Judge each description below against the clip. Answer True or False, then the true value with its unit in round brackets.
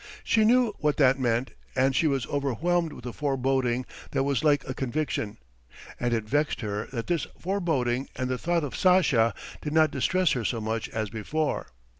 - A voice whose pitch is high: False (135 Hz)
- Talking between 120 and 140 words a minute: False (185 wpm)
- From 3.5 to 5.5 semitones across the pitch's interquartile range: True (4.6 semitones)